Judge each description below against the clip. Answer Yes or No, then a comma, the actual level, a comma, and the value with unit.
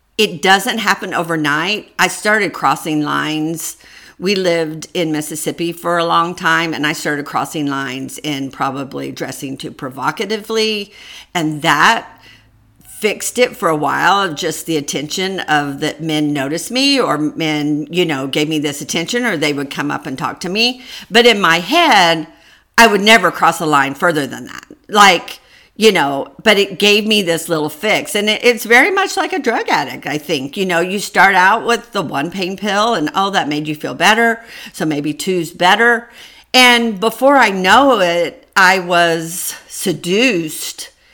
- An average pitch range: No, wide, 5.8 semitones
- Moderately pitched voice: Yes, medium, 170 Hz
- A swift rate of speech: No, average, 180 wpm